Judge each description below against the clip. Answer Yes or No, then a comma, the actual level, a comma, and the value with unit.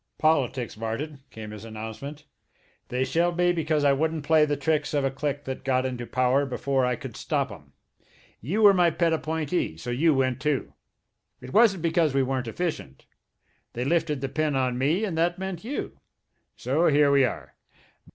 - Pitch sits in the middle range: Yes, medium, 145 Hz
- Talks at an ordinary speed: Yes, average, 180 wpm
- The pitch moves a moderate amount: Yes, average, 4.1 semitones